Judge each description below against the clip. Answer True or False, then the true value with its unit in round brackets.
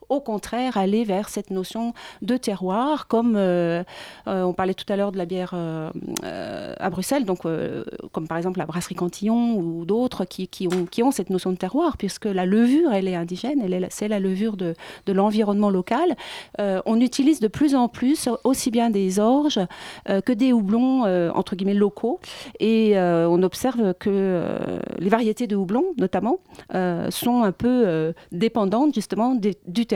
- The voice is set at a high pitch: True (205 Hz)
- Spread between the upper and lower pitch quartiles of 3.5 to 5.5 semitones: True (4.5 semitones)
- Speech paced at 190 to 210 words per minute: True (195 wpm)